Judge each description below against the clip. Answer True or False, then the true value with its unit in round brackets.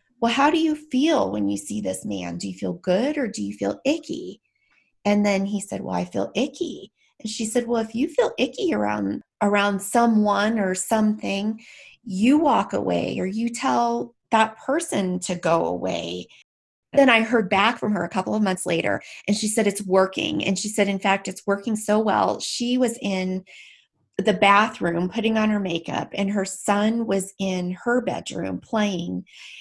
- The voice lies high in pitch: True (205 Hz)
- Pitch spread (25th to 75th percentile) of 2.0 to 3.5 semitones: False (4.1 semitones)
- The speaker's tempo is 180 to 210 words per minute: True (190 wpm)